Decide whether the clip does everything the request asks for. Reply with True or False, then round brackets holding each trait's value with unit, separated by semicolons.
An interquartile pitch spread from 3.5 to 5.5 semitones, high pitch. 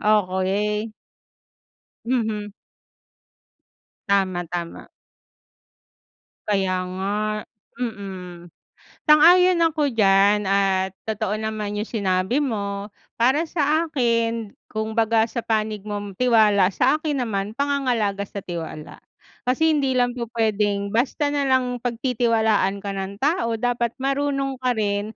True (4.1 semitones; 220 Hz)